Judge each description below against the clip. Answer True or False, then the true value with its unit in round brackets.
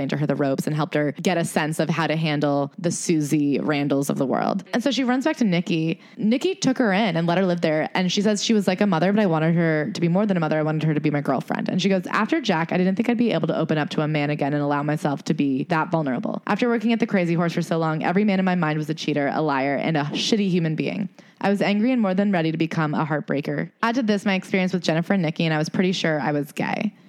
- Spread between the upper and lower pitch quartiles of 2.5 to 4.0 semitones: False (4.9 semitones)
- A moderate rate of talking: False (305 wpm)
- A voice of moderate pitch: True (170 Hz)